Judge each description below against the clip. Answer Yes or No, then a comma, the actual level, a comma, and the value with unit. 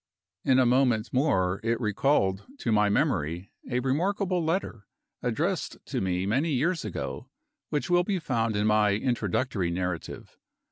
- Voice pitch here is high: No, low, 115 Hz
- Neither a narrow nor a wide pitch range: No, wide, 6.1 semitones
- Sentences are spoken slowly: No, average, 145 wpm